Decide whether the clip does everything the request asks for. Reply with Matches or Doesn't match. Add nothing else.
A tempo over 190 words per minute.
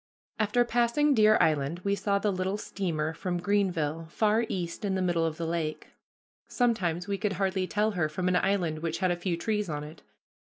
Matches